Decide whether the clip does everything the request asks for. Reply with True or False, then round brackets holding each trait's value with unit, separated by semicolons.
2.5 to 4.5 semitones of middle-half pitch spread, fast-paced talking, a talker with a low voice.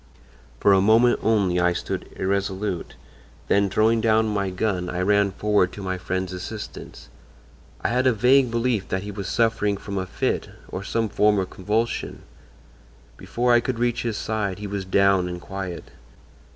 False (2.9 semitones; 170 wpm; 100 Hz)